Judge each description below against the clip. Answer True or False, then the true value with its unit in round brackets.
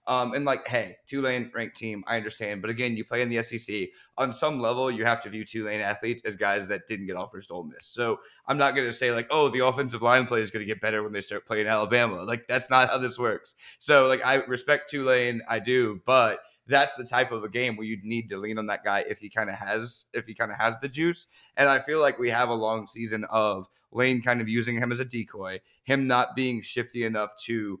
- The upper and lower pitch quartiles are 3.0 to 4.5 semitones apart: False (2.6 semitones)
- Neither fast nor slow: False (255 wpm)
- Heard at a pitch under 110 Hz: False (115 Hz)